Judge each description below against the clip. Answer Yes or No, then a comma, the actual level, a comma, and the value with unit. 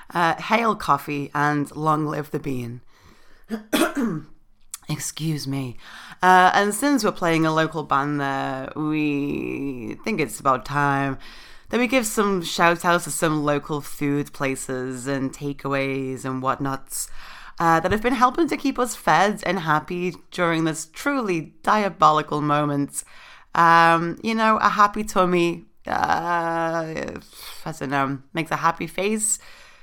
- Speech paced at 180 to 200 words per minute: No, slow, 135 wpm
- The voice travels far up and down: No, average, 4.6 semitones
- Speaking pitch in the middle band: Yes, medium, 155 Hz